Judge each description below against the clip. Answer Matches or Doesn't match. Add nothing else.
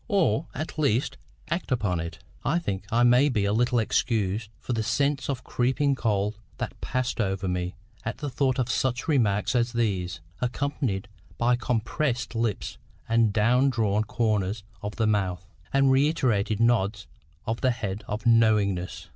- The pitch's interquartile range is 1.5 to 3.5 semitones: Doesn't match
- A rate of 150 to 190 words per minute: Matches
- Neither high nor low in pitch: Doesn't match